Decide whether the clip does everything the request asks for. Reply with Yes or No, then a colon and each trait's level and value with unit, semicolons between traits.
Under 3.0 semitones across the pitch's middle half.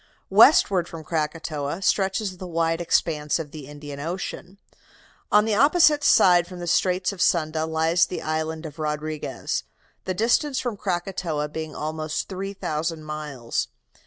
No: average, 3.5 semitones